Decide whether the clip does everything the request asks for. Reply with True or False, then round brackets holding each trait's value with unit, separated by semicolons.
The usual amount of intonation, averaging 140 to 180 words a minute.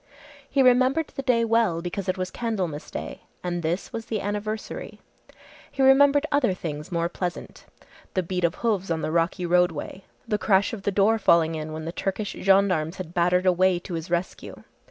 False (4.2 semitones; 190 wpm)